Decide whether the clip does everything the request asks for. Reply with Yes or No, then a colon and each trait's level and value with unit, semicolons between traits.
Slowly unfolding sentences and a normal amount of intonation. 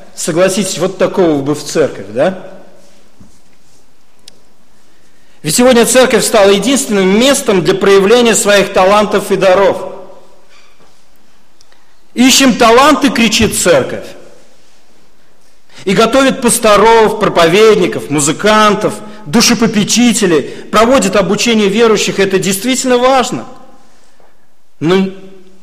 Yes: slow, 85 wpm; average, 3.8 semitones